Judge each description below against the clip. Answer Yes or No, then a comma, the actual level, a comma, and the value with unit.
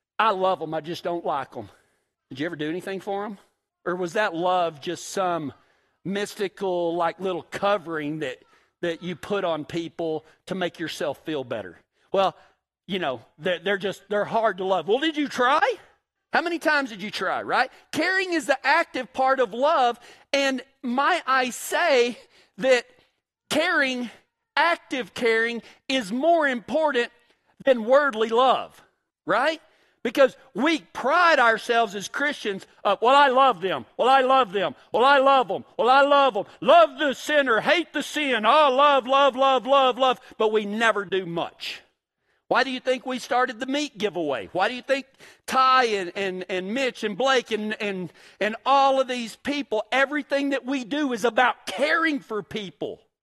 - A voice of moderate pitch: No, high, 245 Hz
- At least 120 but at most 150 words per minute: No, average, 175 wpm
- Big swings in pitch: Yes, wide, 5.8 semitones